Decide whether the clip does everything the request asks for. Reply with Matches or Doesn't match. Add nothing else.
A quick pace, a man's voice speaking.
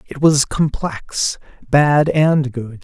Doesn't match